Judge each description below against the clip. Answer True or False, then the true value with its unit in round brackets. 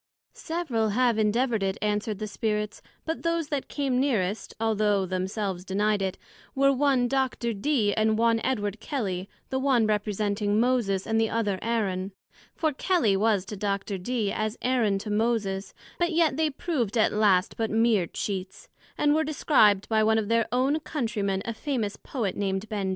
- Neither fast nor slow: True (170 wpm)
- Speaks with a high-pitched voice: True (220 Hz)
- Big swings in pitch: False (4.0 semitones)